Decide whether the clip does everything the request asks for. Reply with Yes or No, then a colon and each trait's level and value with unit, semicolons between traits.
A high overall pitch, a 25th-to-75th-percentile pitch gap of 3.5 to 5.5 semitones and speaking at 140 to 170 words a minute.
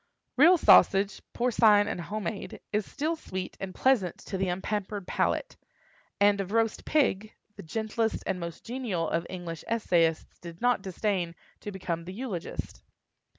Yes: high, 200 Hz; average, 4.0 semitones; average, 150 wpm